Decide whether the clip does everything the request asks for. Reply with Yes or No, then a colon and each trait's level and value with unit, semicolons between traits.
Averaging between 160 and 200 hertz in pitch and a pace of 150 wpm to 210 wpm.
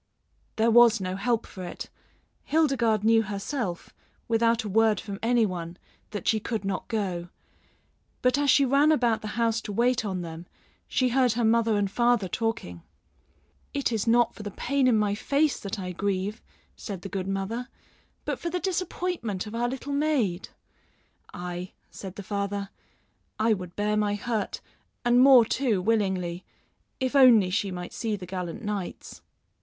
No: high, 220 Hz; average, 170 wpm